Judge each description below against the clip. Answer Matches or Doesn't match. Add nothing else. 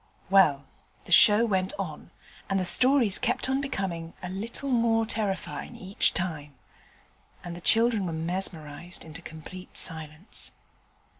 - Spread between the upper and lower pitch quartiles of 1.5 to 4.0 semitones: Doesn't match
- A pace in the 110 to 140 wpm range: Matches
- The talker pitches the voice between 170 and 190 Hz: Matches